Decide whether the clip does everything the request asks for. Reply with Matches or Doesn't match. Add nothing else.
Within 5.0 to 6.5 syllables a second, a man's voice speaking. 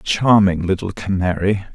Doesn't match